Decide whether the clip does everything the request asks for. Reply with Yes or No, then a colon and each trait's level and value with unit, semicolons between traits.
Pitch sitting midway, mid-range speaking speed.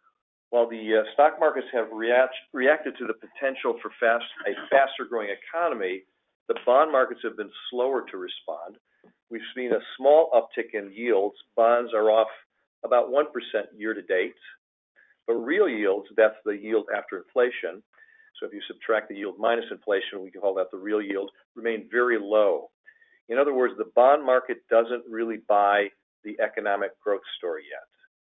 Yes: medium, 155 Hz; average, 170 wpm